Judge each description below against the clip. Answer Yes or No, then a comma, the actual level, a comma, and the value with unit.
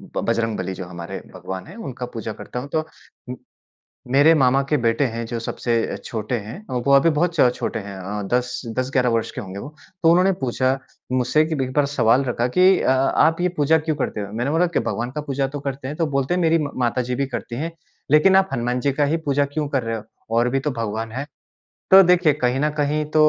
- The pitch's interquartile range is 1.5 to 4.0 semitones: No, average, 4.8 semitones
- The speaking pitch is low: Yes, low, 130 Hz